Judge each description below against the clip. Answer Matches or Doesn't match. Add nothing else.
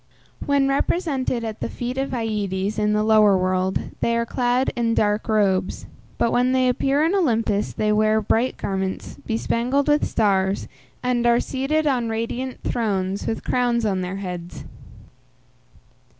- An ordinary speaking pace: Matches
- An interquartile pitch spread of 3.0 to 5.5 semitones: Matches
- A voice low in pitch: Doesn't match